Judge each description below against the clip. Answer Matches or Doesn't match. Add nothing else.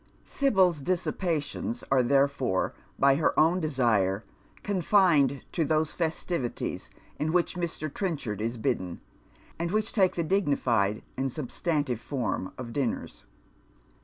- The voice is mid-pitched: Matches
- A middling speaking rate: Doesn't match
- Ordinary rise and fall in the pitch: Doesn't match